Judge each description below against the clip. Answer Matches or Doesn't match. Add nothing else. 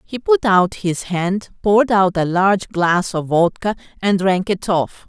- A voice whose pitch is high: Matches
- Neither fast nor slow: Matches